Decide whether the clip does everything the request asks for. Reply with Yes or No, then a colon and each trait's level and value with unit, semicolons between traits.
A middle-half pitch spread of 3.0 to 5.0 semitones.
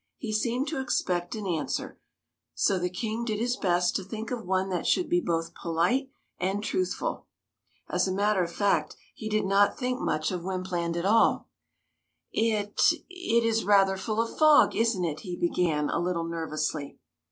Yes: average, 4.5 semitones